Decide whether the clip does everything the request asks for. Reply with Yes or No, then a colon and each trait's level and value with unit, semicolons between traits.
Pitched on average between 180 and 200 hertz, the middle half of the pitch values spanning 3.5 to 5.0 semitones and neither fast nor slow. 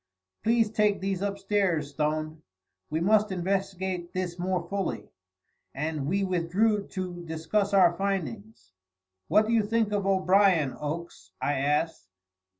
No: medium, 185 Hz; average, 3.9 semitones; slow, 130 wpm